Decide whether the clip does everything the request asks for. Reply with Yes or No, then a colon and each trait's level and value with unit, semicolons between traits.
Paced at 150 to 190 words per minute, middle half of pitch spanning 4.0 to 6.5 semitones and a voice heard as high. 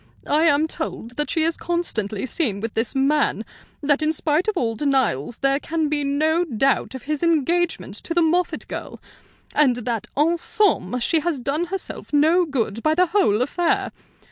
Yes: average, 180 wpm; average, 4.8 semitones; very high, 295 Hz